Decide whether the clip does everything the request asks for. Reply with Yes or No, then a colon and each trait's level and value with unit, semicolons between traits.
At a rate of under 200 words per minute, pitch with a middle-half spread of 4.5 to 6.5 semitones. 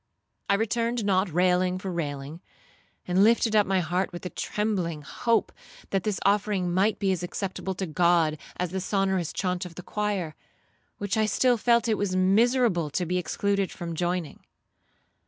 No: average, 170 wpm; average, 2.8 semitones